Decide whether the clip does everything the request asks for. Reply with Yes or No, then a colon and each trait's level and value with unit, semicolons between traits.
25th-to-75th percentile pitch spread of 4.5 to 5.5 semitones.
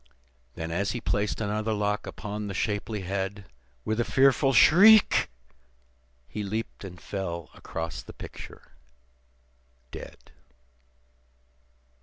No: narrow, 2.6 semitones